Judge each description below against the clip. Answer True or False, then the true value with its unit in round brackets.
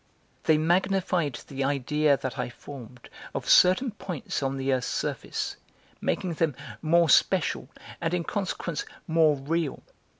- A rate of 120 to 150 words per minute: True (135 wpm)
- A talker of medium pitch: True (155 Hz)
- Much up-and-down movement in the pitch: False (4.0 semitones)